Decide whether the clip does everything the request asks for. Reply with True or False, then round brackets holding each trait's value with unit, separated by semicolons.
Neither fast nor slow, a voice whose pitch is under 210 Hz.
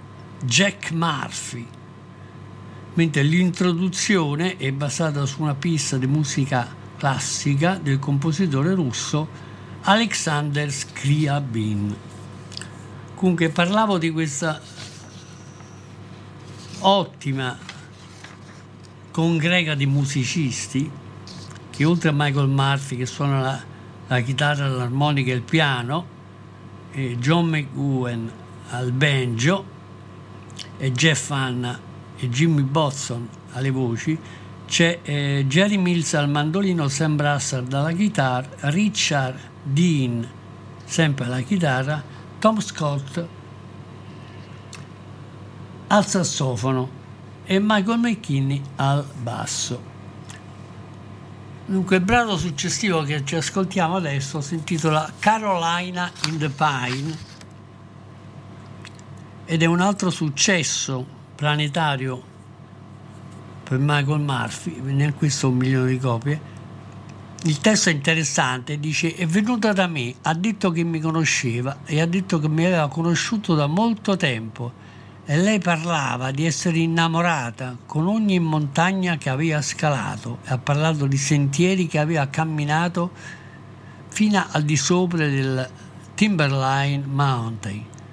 False (105 wpm; 140 Hz)